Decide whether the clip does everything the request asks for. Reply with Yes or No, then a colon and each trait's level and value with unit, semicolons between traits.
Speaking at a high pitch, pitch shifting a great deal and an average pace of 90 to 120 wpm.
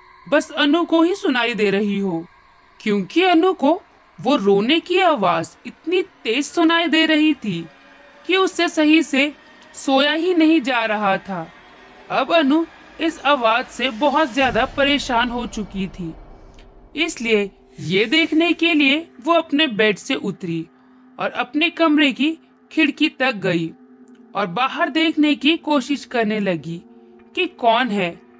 No: very high, 280 Hz; wide, 7.0 semitones; average, 145 wpm